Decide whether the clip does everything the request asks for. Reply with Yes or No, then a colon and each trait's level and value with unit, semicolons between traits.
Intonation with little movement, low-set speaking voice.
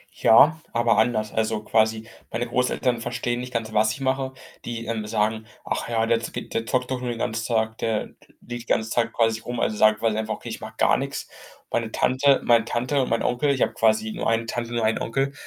Yes: narrow, 1.7 semitones; low, 115 Hz